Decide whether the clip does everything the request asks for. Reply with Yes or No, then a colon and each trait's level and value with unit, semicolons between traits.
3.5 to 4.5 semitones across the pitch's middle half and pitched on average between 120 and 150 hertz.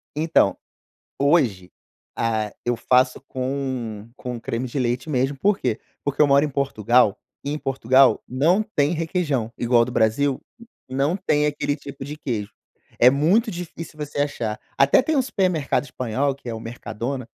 Yes: average, 3.8 semitones; low, 135 Hz